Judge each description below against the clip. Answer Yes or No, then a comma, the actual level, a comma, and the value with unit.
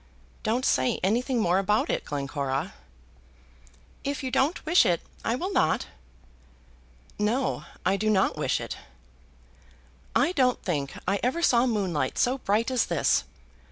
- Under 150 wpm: Yes, average, 140 wpm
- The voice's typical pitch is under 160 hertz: No, high, 215 Hz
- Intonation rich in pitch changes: Yes, wide, 6.1 semitones